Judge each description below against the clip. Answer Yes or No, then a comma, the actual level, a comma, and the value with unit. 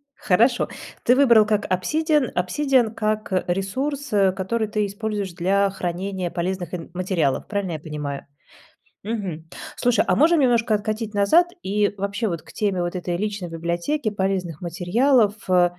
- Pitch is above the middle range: Yes, high, 200 Hz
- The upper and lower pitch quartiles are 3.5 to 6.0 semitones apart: Yes, average, 3.8 semitones